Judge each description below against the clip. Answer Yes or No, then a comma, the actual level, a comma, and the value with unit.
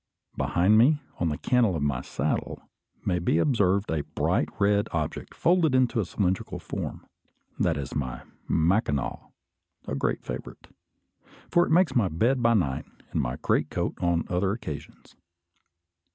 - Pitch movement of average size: No, wide, 6.9 semitones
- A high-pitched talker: No, very low, 95 Hz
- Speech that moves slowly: No, average, 150 wpm